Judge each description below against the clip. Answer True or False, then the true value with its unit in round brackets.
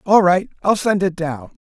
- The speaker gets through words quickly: True (220 wpm)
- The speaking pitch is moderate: True (180 Hz)